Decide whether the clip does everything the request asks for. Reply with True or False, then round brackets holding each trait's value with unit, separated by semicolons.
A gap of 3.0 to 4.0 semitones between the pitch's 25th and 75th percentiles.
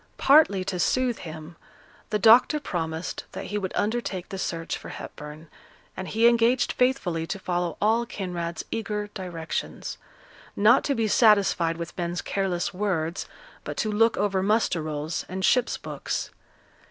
False (4.7 semitones)